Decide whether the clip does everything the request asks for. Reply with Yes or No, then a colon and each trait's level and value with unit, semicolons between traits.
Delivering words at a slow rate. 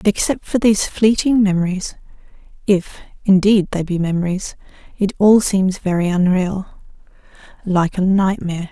Yes: slow, 130 wpm